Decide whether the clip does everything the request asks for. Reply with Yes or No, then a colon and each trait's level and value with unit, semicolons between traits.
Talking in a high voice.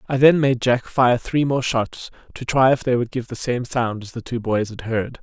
No: low, 125 Hz